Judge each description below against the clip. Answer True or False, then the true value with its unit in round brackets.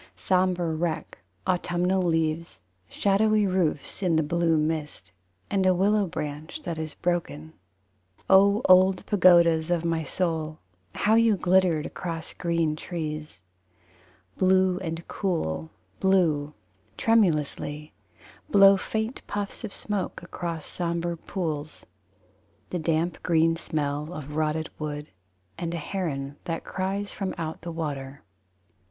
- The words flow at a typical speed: False (120 wpm)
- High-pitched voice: False (170 Hz)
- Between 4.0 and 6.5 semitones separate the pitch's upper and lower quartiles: False (3.2 semitones)